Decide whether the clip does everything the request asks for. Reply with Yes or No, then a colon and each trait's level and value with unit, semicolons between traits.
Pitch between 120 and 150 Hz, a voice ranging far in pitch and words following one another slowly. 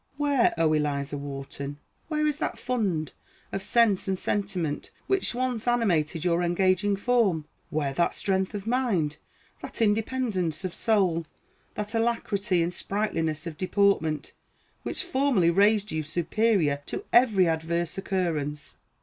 No: high, 190 Hz; wide, 5.7 semitones; slow, 130 wpm